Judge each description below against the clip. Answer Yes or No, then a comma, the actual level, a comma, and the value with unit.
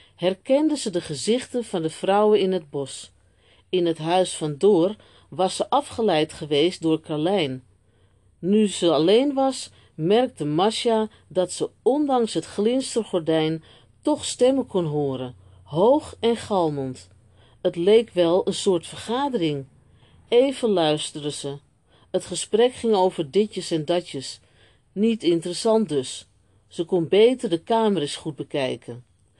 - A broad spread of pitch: Yes, wide, 7.0 semitones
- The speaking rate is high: No, slow, 135 wpm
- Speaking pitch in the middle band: Yes, medium, 175 Hz